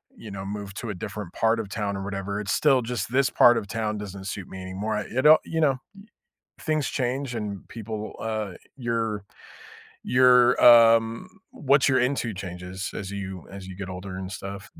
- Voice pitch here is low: Yes, low, 105 Hz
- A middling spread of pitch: Yes, average, 3.7 semitones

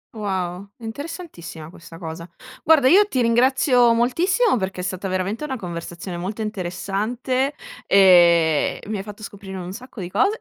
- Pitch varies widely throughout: Yes, wide, 6.0 semitones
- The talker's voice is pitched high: Yes, high, 200 Hz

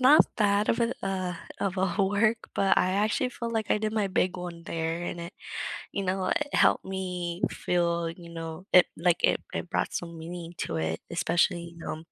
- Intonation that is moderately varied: Yes, average, 3.0 semitones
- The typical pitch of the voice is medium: Yes, medium, 180 Hz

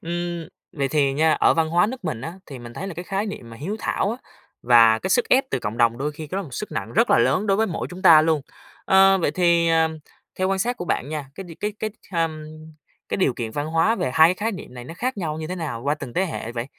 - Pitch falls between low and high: Yes, medium, 165 Hz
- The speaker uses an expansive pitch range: No, average, 5.0 semitones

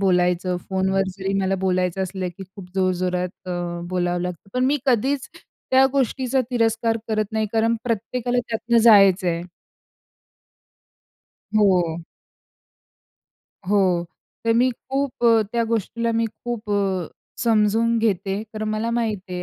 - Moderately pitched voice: No, high, 215 Hz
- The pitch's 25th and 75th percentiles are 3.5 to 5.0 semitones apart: Yes, average, 3.8 semitones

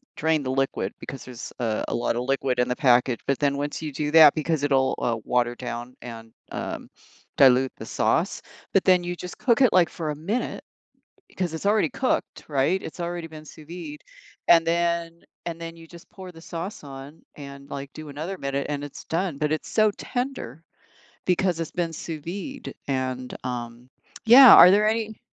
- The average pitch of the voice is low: No, medium, 155 Hz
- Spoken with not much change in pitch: No, average, 4.6 semitones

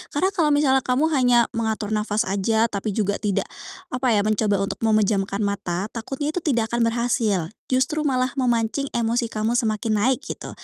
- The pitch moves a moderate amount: Yes, average, 3.3 semitones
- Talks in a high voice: Yes, high, 230 Hz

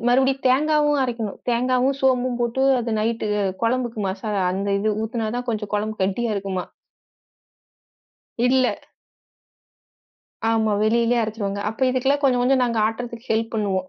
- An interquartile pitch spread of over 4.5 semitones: No, average, 2.9 semitones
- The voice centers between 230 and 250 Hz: Yes, high, 235 Hz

